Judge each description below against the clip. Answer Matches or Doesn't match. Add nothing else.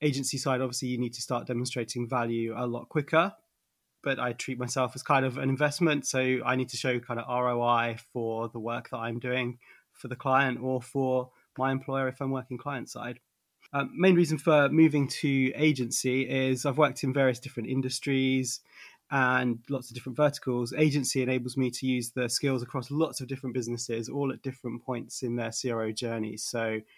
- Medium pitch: Doesn't match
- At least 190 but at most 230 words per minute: Matches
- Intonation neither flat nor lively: Doesn't match